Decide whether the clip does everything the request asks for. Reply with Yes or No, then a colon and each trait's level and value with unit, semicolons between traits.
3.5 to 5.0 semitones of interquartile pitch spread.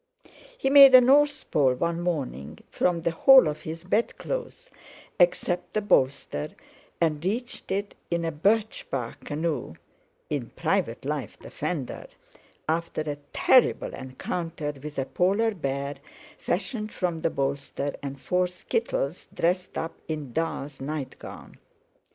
No: wide, 5.6 semitones